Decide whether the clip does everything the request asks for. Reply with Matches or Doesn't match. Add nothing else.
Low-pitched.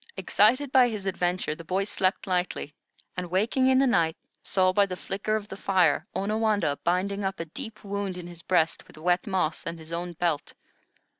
Doesn't match